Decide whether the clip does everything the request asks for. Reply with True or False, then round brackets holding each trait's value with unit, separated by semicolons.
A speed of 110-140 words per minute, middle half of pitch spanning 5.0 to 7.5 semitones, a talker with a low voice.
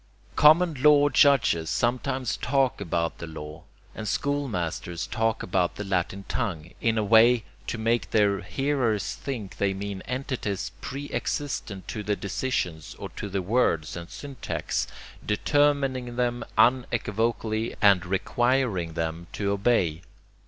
True (135 wpm; 5.3 semitones; 110 Hz)